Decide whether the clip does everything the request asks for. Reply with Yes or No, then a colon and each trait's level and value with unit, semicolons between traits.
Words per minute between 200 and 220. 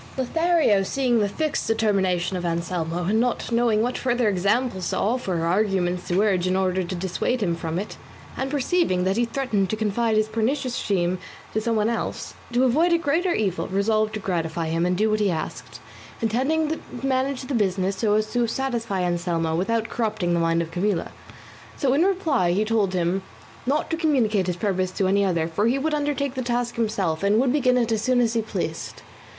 Yes: fast, 205 wpm